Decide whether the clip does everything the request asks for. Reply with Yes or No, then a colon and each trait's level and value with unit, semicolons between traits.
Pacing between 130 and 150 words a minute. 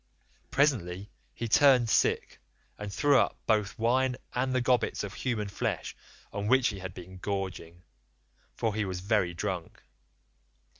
Yes: average, 145 wpm